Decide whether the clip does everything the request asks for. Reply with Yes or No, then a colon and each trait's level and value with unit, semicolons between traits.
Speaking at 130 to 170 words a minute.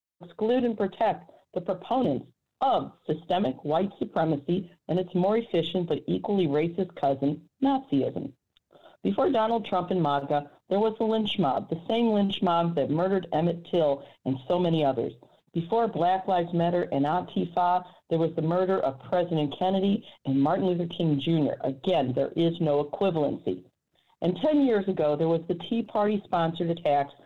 Yes: average, 165 wpm